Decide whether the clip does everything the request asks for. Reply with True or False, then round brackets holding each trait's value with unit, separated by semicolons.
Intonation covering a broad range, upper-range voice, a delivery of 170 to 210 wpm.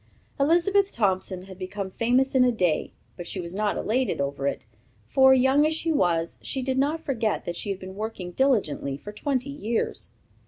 True (6.4 semitones; 220 Hz; 190 wpm)